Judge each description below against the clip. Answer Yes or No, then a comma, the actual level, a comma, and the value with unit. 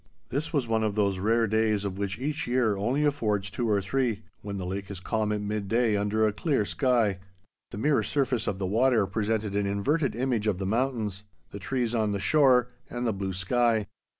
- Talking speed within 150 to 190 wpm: No, fast, 205 wpm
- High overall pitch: No, low, 110 Hz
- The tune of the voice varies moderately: Yes, average, 3.5 semitones